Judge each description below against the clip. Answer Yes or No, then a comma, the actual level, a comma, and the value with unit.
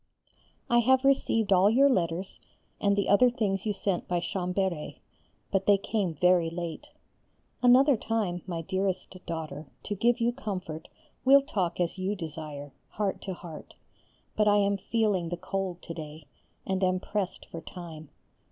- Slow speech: No, average, 160 wpm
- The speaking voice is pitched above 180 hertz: Yes, high, 190 Hz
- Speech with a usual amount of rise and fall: Yes, average, 3.6 semitones